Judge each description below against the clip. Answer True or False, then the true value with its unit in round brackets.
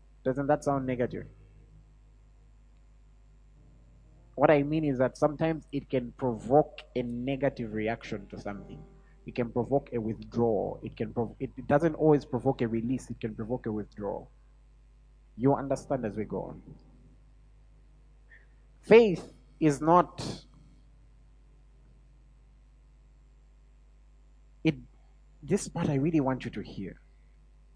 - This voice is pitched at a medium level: False (130 Hz)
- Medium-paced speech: False (120 wpm)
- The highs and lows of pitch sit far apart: False (3.8 semitones)